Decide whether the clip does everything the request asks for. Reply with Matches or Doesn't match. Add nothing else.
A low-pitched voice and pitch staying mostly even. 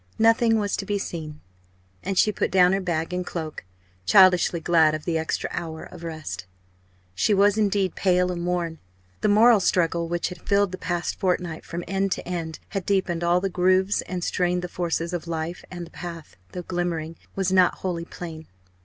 Doesn't match